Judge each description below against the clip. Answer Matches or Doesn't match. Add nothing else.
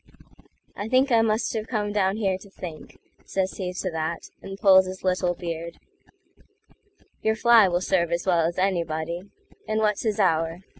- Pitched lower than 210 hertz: Matches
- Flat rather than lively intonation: Doesn't match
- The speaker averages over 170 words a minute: Doesn't match